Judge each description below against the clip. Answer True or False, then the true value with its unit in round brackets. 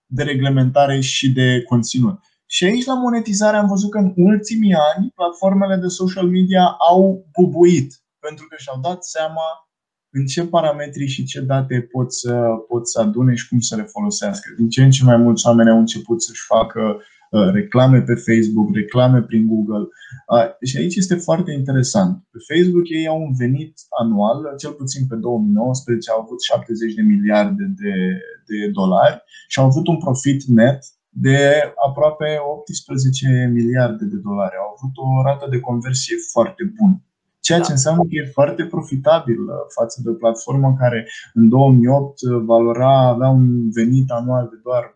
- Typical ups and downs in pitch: False (6.4 semitones)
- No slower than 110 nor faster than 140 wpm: False (165 wpm)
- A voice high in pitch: False (135 Hz)